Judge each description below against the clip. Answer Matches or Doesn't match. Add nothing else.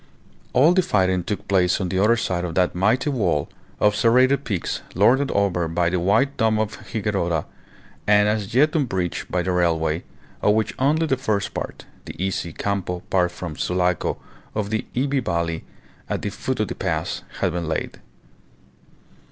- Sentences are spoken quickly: Doesn't match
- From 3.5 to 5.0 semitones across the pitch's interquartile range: Matches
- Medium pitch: Doesn't match